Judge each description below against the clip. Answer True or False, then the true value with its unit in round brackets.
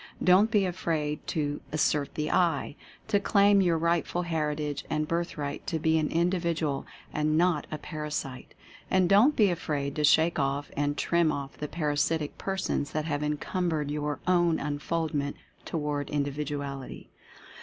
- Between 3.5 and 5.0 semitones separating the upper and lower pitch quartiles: False (2.8 semitones)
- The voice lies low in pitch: False (155 Hz)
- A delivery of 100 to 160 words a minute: True (155 wpm)